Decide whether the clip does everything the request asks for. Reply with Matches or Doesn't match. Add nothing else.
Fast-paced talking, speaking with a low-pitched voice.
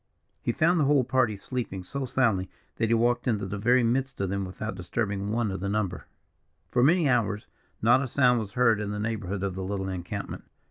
Matches